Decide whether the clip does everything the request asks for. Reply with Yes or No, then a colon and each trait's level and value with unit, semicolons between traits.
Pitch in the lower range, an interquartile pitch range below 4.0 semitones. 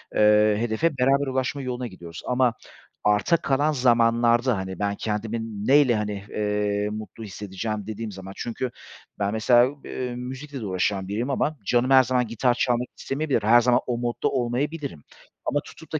Yes: low, 120 Hz; average, 3.6 semitones